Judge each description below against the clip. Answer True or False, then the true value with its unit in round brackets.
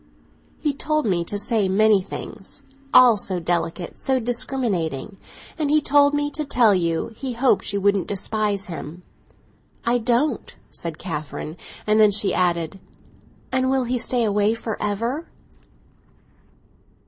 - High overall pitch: True (215 Hz)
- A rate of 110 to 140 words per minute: True (135 wpm)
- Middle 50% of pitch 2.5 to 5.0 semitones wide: False (5.4 semitones)